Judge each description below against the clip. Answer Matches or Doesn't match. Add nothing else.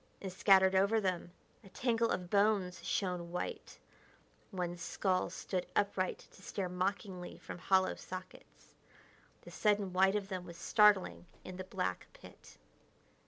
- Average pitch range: Doesn't match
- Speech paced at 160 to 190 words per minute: Doesn't match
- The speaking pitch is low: Doesn't match